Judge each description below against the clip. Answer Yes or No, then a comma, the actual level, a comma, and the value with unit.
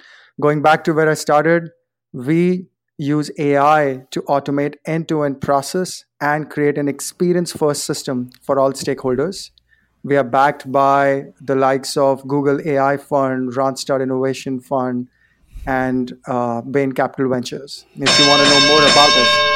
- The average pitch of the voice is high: No, medium, 140 Hz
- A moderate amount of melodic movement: No, narrow, 1.9 semitones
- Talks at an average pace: Yes, average, 145 wpm